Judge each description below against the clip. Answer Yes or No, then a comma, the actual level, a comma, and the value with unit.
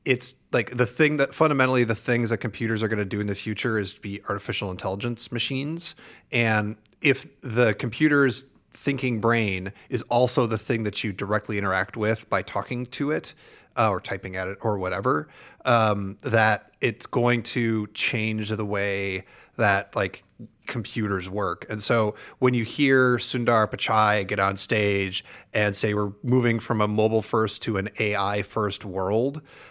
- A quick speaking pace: No, average, 170 wpm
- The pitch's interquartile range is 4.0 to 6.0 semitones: No, average, 3.1 semitones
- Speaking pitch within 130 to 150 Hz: No, low, 110 Hz